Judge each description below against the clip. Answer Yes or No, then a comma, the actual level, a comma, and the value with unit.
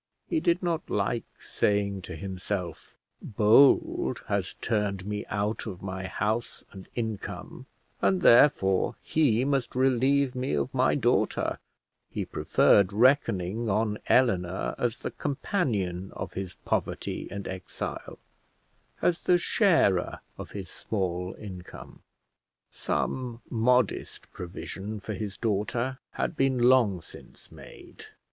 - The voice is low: Yes, low, 105 Hz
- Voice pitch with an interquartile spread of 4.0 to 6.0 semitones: Yes, average, 5.0 semitones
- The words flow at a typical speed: No, slow, 120 wpm